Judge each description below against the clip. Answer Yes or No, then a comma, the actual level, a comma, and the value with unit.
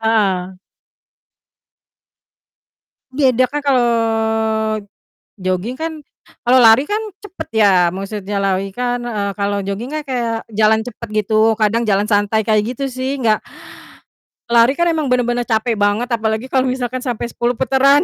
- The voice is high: Yes, high, 230 Hz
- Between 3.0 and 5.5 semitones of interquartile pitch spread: Yes, average, 3.4 semitones